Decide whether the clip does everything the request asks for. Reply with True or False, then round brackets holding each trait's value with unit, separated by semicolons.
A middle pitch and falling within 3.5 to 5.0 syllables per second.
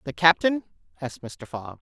False (150 Hz; 5.3 syllables/s)